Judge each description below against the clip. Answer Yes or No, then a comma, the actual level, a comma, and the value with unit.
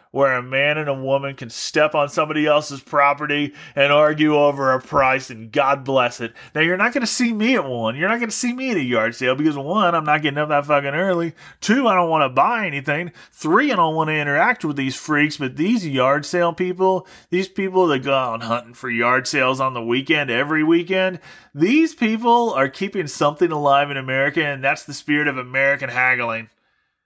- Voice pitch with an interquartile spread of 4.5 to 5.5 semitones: Yes, average, 4.9 semitones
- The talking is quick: Yes, fast, 220 wpm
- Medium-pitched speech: Yes, medium, 150 Hz